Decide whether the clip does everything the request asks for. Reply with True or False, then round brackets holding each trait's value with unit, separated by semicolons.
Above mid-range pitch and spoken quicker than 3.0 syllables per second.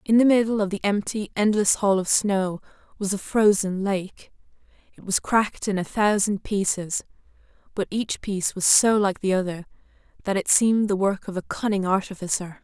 True (200 Hz; 5.1 syllables/s)